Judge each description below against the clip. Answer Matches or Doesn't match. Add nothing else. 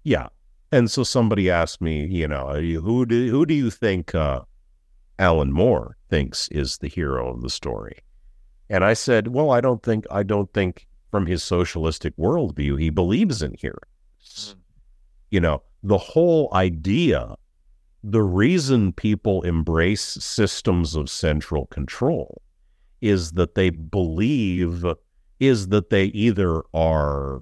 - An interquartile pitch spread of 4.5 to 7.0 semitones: Matches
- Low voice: Matches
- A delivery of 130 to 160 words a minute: Matches